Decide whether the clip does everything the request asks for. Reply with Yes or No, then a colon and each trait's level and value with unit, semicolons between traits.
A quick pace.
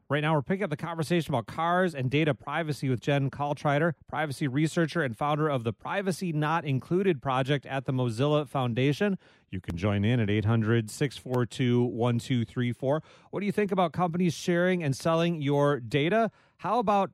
No: average, 170 wpm